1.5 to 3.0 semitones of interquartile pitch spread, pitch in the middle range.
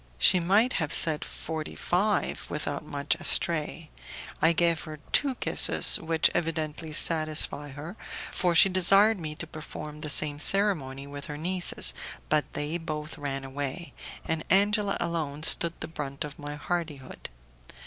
Yes: average, 2.7 semitones; medium, 160 Hz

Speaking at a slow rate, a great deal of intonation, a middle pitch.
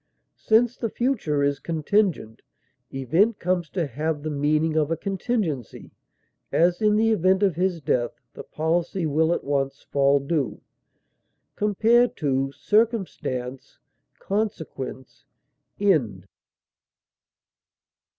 Yes: slow, 105 wpm; wide, 6.2 semitones; medium, 160 Hz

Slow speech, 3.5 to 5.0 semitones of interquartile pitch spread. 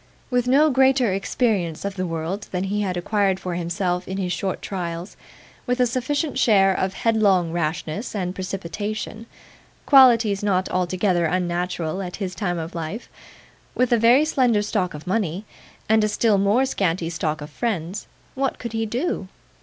No: average, 165 wpm; average, 4.3 semitones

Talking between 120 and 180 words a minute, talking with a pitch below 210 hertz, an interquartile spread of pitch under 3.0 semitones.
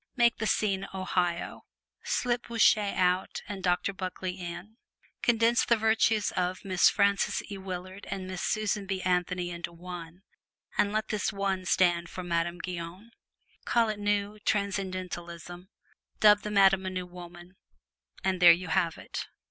Yes: average, 150 wpm; medium, 185 Hz; narrow, 2.5 semitones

